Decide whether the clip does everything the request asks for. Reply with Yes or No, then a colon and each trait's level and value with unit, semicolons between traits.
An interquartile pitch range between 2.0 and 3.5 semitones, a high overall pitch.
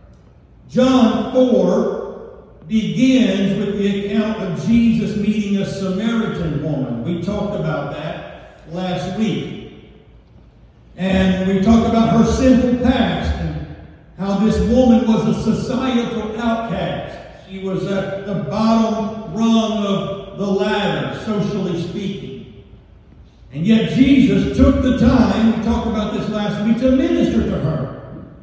Yes: average, 3.0 semitones; high, 210 Hz